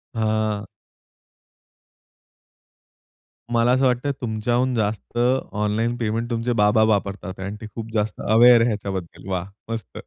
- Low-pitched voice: Yes, low, 110 Hz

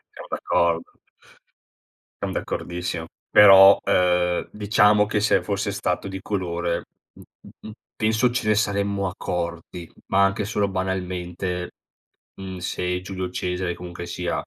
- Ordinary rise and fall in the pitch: No, narrow, 2.3 semitones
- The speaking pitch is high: No, very low, 95 Hz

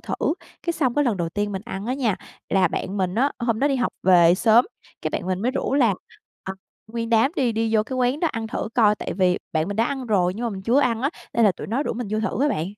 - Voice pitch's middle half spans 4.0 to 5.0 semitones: Yes, average, 4.5 semitones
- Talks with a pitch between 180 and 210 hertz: No, high, 225 Hz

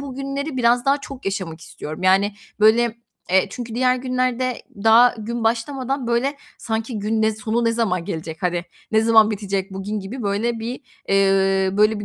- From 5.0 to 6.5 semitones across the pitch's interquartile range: No, average, 3.8 semitones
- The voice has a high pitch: Yes, high, 225 Hz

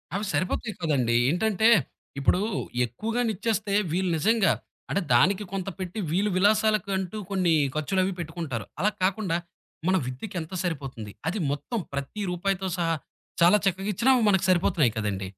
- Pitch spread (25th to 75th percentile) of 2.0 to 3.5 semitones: No, average, 4.4 semitones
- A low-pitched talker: No, medium, 185 Hz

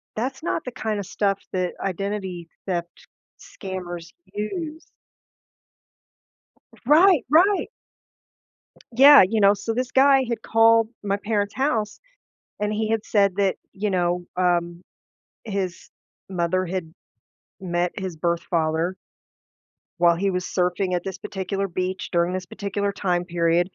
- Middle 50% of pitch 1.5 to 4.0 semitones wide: Yes, average, 3.5 semitones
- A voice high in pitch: Yes, high, 195 Hz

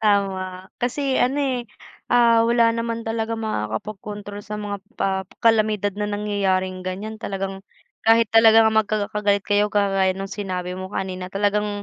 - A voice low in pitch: No, high, 205 Hz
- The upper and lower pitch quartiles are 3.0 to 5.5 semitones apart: No, narrow, 2.6 semitones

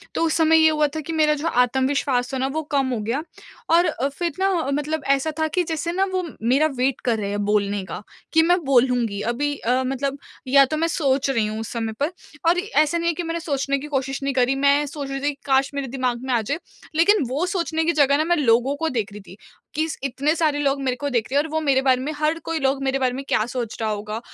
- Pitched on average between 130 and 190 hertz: No, very high, 275 Hz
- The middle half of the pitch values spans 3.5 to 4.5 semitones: Yes, average, 3.9 semitones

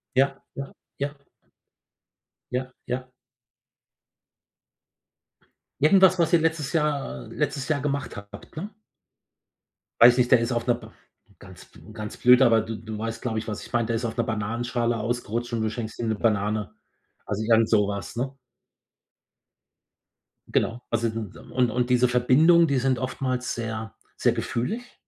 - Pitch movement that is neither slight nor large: Yes, average, 3.1 semitones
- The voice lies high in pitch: No, low, 120 Hz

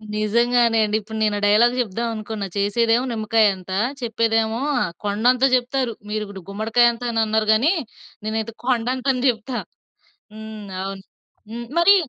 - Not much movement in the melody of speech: Yes, narrow, 2.0 semitones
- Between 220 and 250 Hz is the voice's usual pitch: Yes, high, 225 Hz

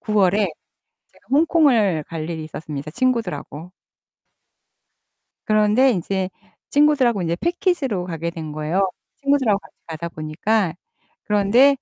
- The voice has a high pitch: Yes, high, 200 Hz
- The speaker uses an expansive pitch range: Yes, wide, 7.7 semitones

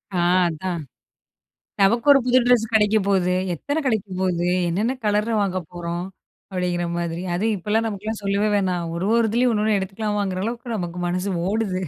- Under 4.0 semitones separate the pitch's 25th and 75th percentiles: Yes, average, 3.5 semitones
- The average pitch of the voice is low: No, high, 200 Hz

